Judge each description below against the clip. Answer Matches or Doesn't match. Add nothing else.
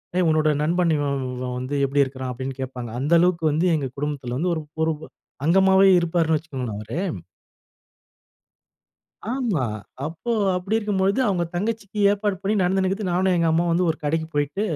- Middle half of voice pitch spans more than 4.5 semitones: Matches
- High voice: Doesn't match